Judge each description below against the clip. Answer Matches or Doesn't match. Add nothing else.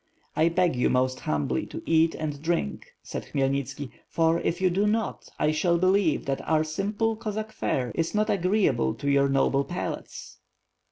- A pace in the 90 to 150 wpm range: Doesn't match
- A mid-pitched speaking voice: Matches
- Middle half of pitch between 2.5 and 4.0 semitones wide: Doesn't match